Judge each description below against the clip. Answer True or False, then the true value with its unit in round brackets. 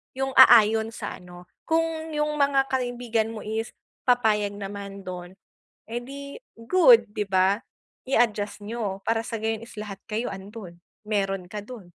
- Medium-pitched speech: False (220 Hz)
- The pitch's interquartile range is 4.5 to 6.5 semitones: False (3.6 semitones)